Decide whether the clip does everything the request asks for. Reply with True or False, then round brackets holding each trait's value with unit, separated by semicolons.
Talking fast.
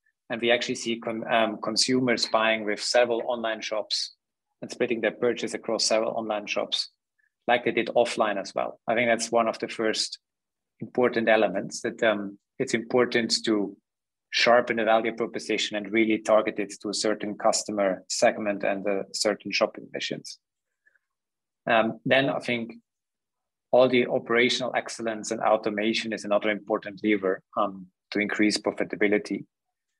False (155 wpm)